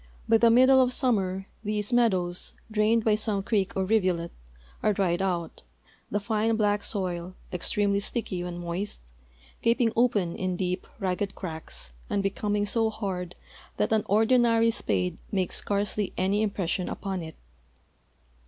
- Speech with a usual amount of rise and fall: Yes, average, 3.3 semitones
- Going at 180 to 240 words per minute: No, average, 145 wpm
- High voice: Yes, high, 200 Hz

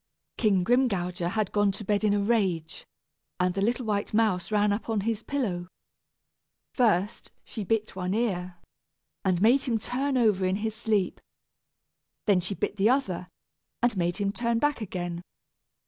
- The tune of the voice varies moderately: Yes, average, 3.6 semitones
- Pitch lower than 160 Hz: No, high, 205 Hz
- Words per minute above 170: No, average, 165 wpm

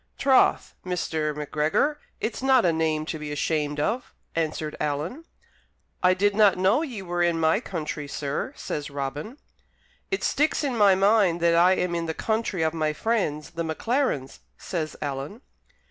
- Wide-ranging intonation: Yes, wide, 5.8 semitones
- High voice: No, medium, 170 Hz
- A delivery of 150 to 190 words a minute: Yes, average, 160 wpm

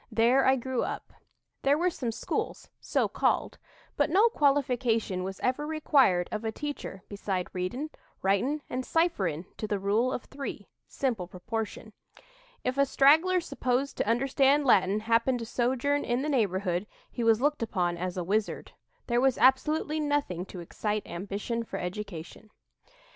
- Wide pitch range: Yes, wide, 5.8 semitones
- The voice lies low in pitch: No, high, 235 Hz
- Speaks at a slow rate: No, average, 155 wpm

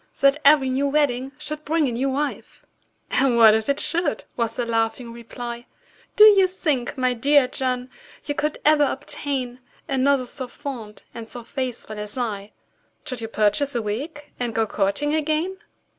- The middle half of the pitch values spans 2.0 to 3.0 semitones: No, average, 3.8 semitones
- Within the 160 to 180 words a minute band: Yes, average, 170 wpm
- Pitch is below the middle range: No, very high, 260 Hz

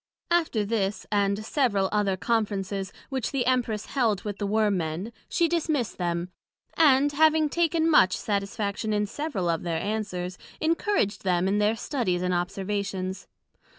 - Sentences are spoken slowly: No, average, 150 wpm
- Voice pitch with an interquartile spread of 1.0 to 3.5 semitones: No, average, 5.2 semitones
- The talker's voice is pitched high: Yes, high, 210 Hz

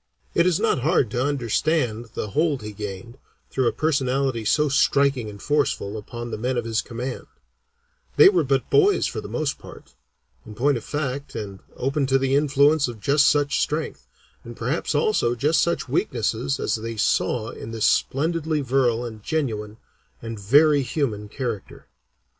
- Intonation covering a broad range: No, average, 4.3 semitones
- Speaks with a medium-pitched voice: No, low, 130 Hz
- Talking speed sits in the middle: Yes, average, 170 wpm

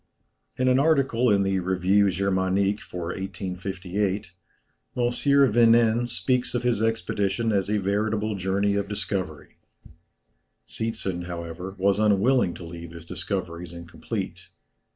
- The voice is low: Yes, low, 100 Hz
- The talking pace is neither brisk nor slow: No, slow, 120 wpm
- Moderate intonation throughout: Yes, average, 3.4 semitones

